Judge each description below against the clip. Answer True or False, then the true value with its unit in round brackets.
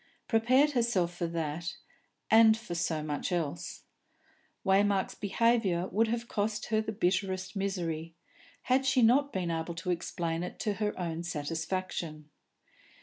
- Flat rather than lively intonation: False (4.7 semitones)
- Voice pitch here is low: False (185 Hz)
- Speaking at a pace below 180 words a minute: True (140 wpm)